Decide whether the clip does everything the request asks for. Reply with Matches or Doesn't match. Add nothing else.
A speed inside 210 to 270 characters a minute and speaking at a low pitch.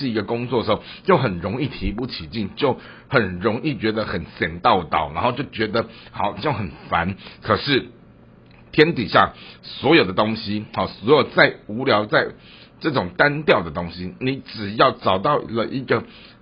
Matches